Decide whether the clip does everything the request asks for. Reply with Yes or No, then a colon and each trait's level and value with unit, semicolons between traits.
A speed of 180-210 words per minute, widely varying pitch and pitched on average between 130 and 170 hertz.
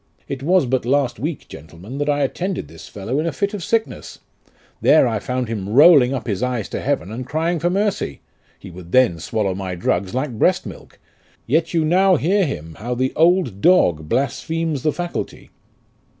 Yes: average, 190 wpm; wide, 7.2 semitones; low, 135 Hz